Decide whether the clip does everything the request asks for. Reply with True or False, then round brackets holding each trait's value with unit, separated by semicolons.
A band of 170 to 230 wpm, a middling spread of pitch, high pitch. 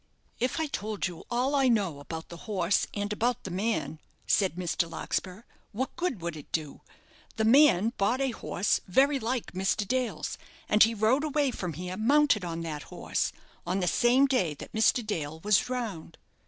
False (180 wpm; 6.1 semitones; 210 Hz)